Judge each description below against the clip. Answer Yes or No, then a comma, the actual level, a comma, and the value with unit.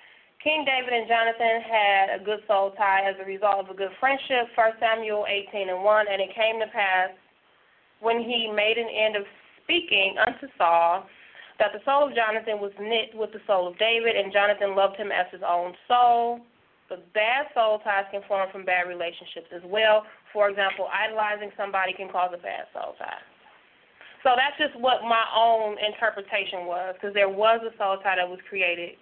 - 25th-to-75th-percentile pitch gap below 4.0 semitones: Yes, average, 2.8 semitones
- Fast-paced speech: No, average, 190 wpm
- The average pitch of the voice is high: Yes, high, 210 Hz